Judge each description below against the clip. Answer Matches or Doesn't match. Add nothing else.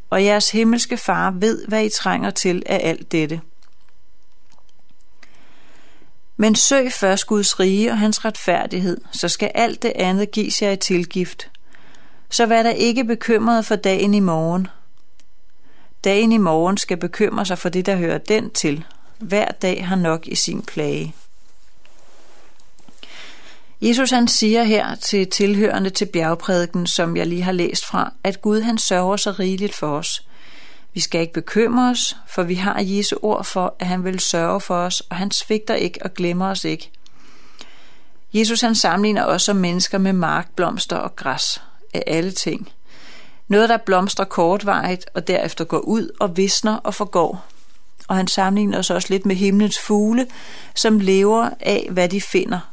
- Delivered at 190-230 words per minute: Doesn't match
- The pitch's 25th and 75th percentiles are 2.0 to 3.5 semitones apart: Matches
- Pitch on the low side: Doesn't match